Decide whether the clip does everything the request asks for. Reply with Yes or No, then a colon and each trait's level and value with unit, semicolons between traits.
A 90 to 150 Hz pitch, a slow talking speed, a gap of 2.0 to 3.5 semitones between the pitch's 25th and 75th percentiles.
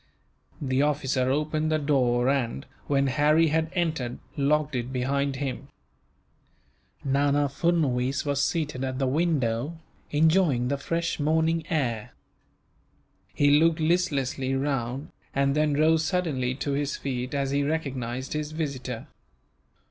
Yes: medium, 140 Hz; slow, 125 wpm; average, 2.9 semitones